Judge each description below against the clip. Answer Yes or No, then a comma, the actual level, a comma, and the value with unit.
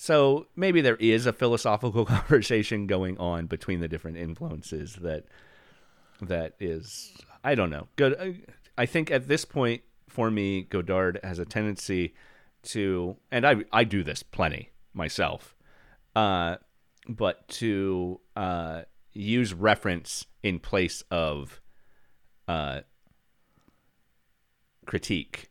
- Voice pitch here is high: No, low, 100 Hz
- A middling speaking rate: No, slow, 120 wpm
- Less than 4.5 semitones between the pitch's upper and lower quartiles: No, wide, 5.4 semitones